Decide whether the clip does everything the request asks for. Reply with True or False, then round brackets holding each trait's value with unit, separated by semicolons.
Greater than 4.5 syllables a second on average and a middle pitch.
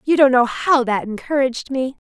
False (5.3 syllables/s; 260 Hz)